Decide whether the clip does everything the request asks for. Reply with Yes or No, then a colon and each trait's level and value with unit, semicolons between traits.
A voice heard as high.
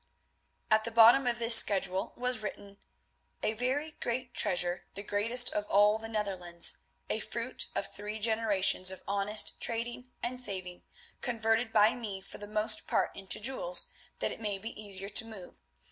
Yes: high, 215 Hz